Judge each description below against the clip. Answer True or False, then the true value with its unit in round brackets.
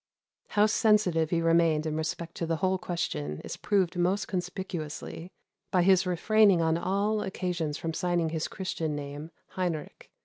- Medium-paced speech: True (150 wpm)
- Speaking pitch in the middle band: True (175 Hz)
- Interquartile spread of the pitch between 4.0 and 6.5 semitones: False (2.7 semitones)